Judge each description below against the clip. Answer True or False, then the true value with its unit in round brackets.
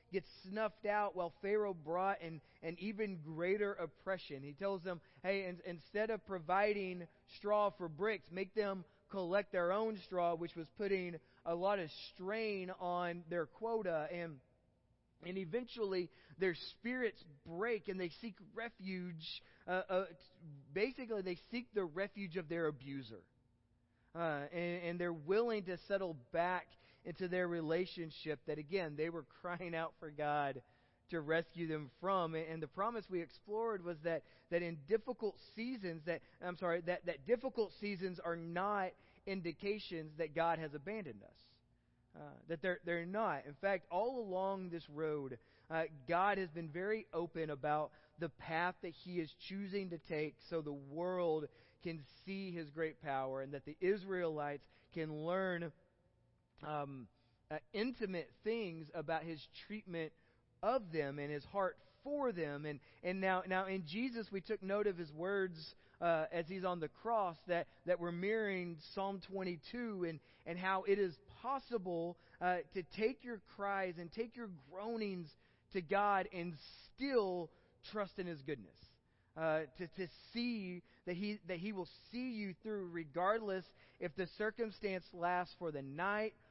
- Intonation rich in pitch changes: False (3.7 semitones)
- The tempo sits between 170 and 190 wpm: False (160 wpm)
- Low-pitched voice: False (180 Hz)